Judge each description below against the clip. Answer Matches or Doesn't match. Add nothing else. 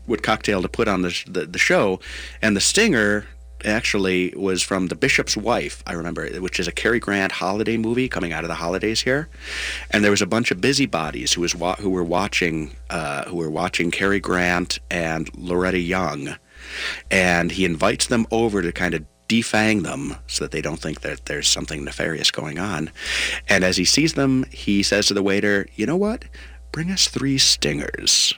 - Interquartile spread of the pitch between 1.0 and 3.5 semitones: Doesn't match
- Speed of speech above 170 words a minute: Matches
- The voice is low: Matches